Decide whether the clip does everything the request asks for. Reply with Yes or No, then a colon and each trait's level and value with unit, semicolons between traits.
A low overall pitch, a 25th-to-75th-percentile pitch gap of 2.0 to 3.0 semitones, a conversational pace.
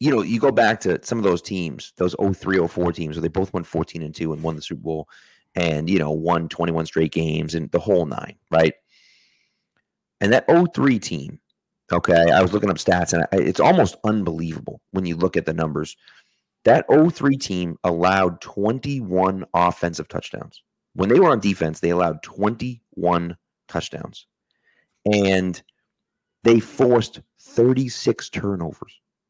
No: very low, 90 Hz; average, 3.8 semitones; average, 165 wpm